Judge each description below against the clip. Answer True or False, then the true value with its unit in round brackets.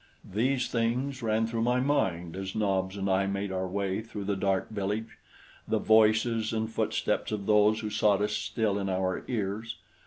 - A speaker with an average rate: True (180 wpm)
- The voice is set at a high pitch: False (105 Hz)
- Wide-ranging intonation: False (2.5 semitones)